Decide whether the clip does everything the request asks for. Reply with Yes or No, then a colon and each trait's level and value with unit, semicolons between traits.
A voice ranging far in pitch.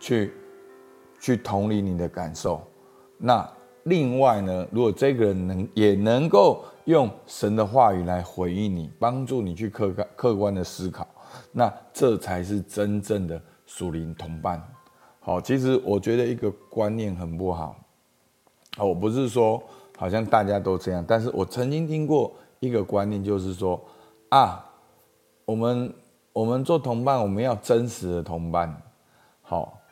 No: average, 5.0 semitones